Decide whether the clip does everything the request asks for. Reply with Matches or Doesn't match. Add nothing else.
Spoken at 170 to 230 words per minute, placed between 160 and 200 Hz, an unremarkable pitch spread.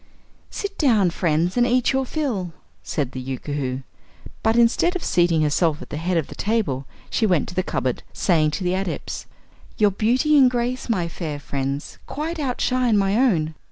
Doesn't match